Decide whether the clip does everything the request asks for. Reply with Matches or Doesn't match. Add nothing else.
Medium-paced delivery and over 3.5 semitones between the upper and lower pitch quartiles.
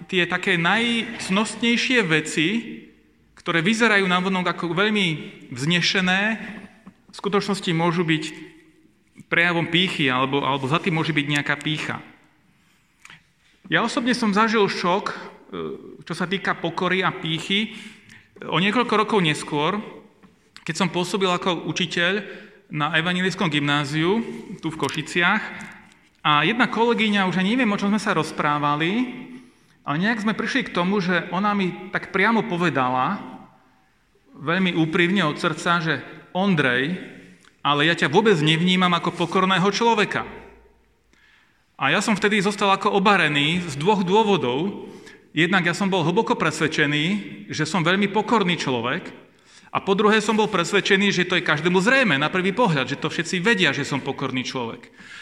Matches